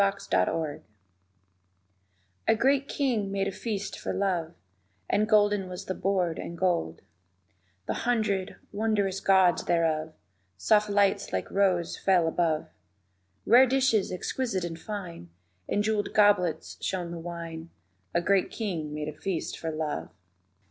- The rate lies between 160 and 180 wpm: No, slow, 135 wpm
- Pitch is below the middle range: No, high, 190 Hz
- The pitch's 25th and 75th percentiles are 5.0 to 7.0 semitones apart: No, average, 3.8 semitones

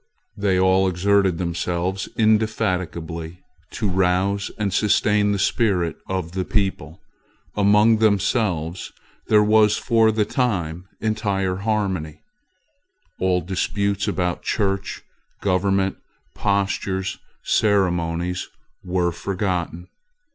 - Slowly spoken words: Yes, slow, 95 wpm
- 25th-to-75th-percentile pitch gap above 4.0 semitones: No, narrow, 2.5 semitones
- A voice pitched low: Yes, very low, 95 Hz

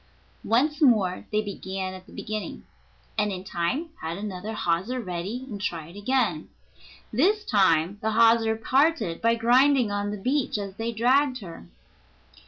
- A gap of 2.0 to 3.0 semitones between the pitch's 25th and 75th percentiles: No, average, 4.9 semitones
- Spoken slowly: No, average, 150 wpm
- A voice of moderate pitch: No, high, 215 Hz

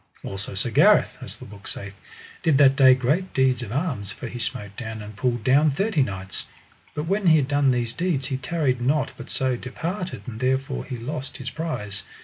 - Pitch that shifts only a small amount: No, average, 4.3 semitones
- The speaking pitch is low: Yes, low, 130 Hz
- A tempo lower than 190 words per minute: No, fast, 205 wpm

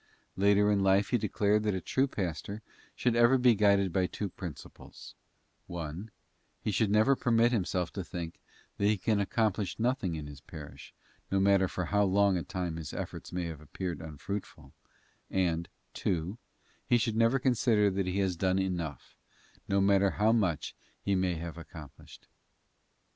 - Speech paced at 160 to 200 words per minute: Yes, average, 165 wpm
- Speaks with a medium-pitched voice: No, very low, 95 Hz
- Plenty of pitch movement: No, average, 3.5 semitones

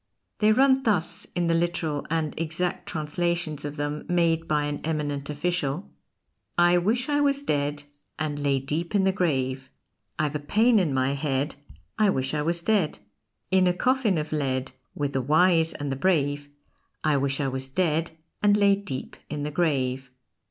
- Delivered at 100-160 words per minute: No, average, 175 wpm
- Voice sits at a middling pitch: Yes, medium, 155 Hz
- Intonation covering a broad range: No, average, 3.8 semitones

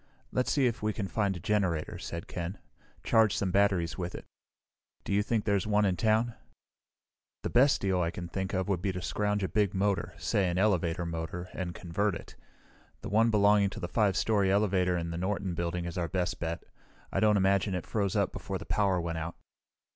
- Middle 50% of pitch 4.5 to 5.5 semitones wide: No, average, 3.0 semitones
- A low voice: Yes, very low, 95 Hz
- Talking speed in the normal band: No, fast, 210 wpm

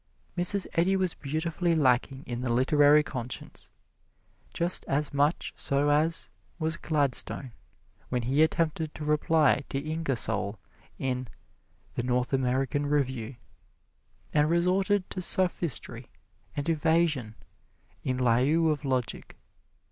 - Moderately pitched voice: Yes, medium, 145 Hz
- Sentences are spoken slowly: Yes, slow, 115 wpm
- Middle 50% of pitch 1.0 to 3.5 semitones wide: No, average, 4.0 semitones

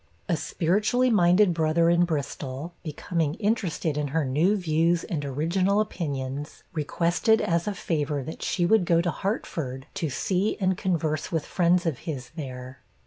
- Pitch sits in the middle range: Yes, medium, 165 Hz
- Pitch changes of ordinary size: Yes, average, 3.7 semitones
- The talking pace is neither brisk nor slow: Yes, average, 155 wpm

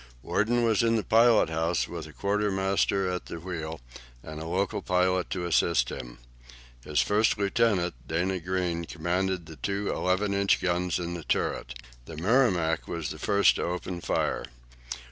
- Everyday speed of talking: Yes, average, 165 wpm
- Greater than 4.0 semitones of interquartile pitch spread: No, average, 3.1 semitones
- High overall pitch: No, very low, 90 Hz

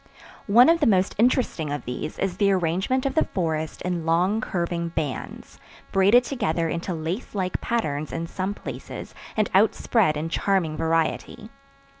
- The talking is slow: No, average, 160 wpm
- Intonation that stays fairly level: No, average, 4.3 semitones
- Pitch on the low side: No, medium, 180 Hz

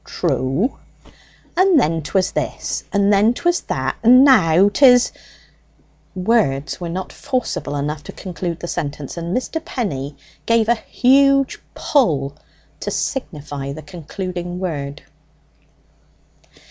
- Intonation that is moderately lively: No, wide, 8.5 semitones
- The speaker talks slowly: Yes, slow, 120 wpm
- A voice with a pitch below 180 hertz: No, medium, 185 Hz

